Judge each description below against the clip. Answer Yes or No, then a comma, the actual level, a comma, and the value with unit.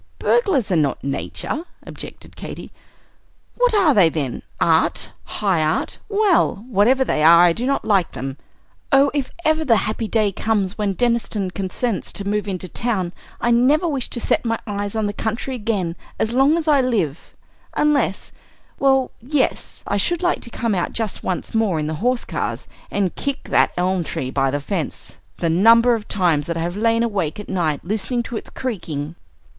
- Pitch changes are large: Yes, wide, 6.0 semitones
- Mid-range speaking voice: No, high, 210 Hz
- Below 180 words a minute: No, average, 185 wpm